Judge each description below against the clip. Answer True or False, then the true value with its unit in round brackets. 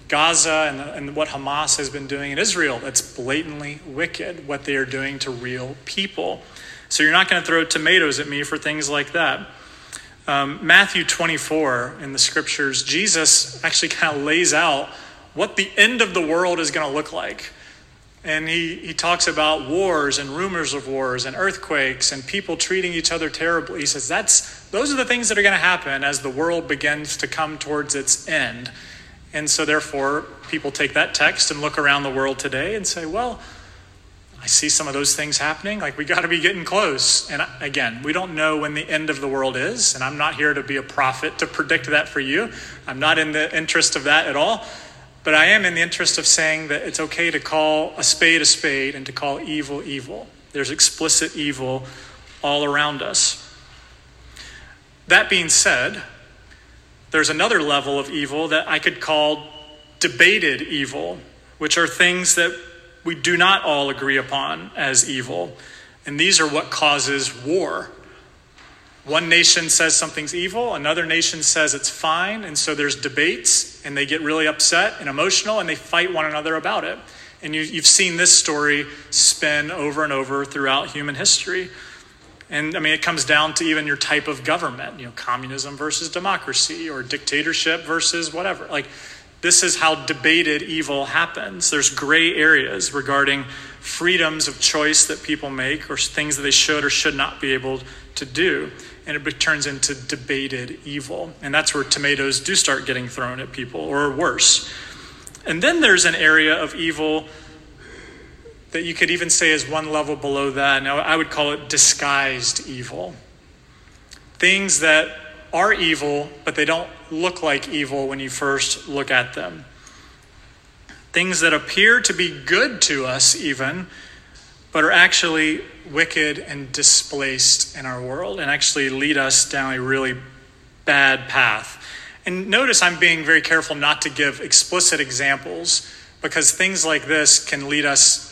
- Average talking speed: True (180 wpm)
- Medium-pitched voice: True (150 Hz)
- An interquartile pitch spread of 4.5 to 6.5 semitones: False (2.6 semitones)